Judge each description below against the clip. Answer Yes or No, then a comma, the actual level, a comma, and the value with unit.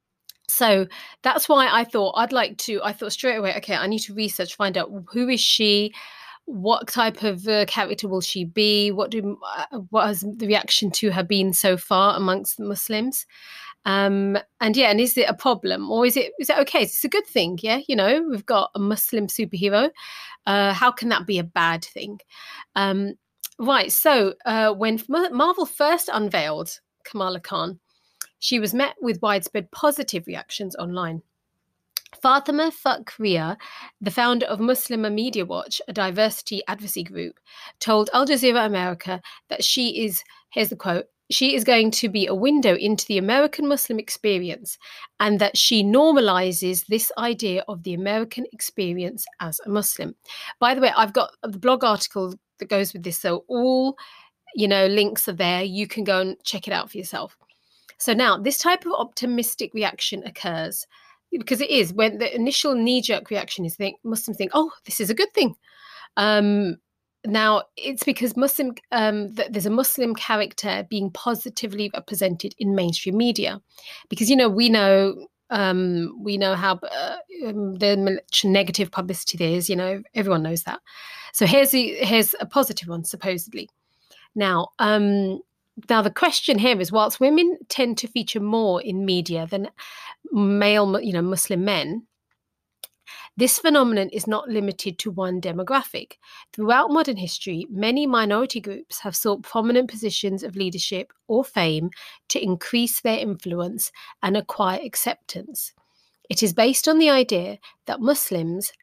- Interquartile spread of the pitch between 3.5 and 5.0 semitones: Yes, average, 4.2 semitones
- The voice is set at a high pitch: Yes, high, 215 Hz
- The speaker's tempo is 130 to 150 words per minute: No, average, 165 wpm